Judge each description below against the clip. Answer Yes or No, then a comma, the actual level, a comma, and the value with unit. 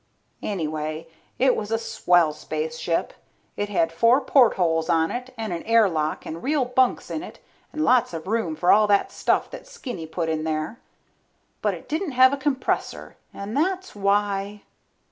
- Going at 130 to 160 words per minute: No, average, 170 wpm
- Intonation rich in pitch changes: Yes, wide, 7.7 semitones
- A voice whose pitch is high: Yes, high, 205 Hz